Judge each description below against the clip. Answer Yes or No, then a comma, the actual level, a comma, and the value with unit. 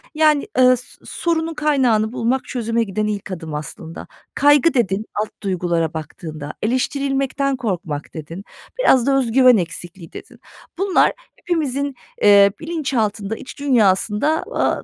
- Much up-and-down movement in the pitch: Yes, wide, 6.5 semitones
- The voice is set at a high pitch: Yes, high, 230 Hz